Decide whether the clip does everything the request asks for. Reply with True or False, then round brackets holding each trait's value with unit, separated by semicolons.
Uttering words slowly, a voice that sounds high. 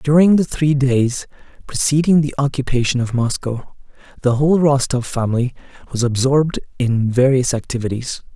False (130 wpm; 130 Hz)